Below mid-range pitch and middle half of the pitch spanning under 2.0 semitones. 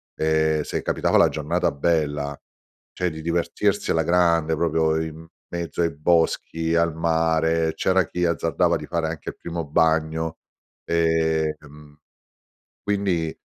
Yes: very low, 80 Hz; narrow, 1.2 semitones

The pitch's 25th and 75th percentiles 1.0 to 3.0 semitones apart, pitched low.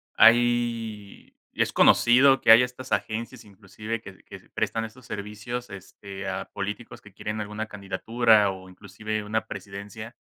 Yes: narrow, 2.6 semitones; low, 110 Hz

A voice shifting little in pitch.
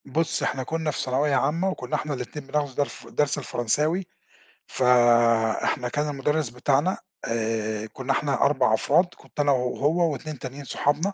No: average, 3.3 semitones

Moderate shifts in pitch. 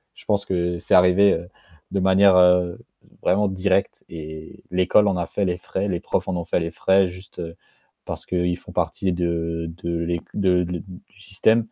No: narrow, 1.8 semitones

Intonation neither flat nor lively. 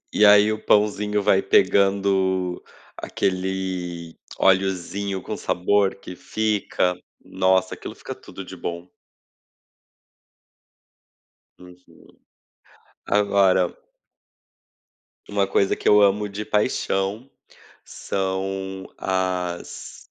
No: narrow, 1.6 semitones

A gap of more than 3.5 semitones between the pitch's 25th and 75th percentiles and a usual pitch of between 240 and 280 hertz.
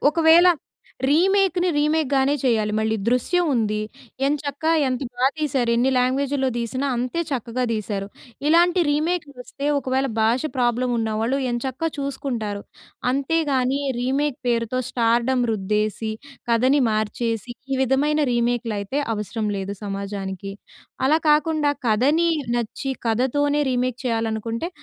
Yes: average, 4.2 semitones; very high, 255 Hz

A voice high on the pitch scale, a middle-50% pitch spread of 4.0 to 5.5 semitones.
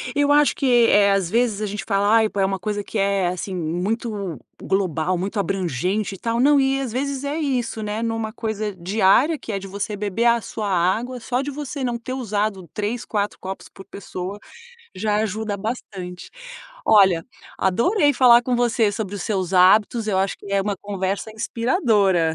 No: high, 210 Hz; average, 3.5 semitones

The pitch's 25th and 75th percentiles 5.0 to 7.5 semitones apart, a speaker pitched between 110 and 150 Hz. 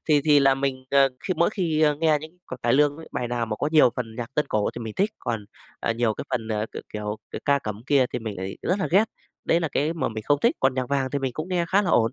Yes: average, 5.3 semitones; low, 135 Hz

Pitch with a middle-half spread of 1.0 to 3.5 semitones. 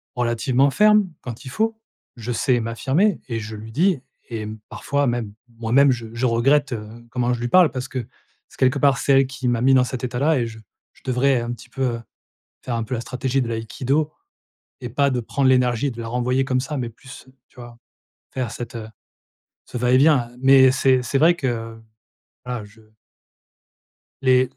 Yes: narrow, 2.4 semitones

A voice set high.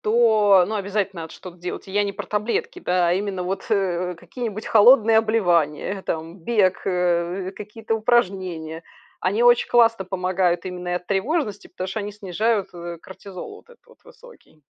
Yes: high, 195 Hz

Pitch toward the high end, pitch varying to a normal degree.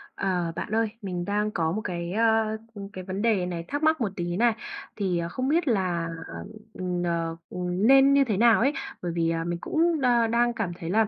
Yes: high, 200 Hz; average, 5.0 semitones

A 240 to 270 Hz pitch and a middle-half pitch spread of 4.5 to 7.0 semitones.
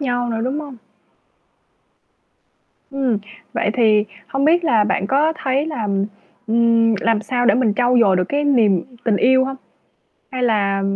No: high, 245 Hz; average, 3.9 semitones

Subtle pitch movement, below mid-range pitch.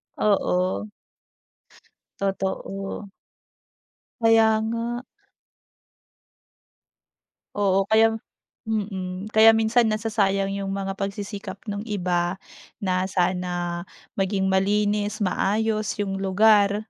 No: narrow, 2.0 semitones; high, 200 Hz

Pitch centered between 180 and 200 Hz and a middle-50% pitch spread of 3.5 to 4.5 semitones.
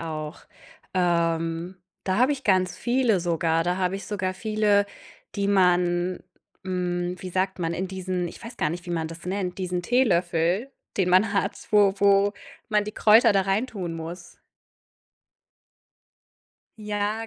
No: medium, 185 Hz; average, 2.7 semitones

